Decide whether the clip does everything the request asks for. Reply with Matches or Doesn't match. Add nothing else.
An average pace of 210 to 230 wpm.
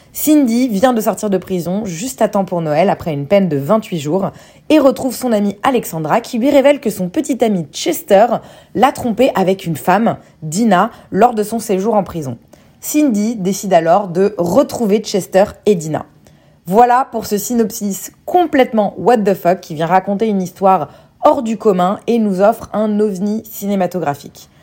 Doesn't match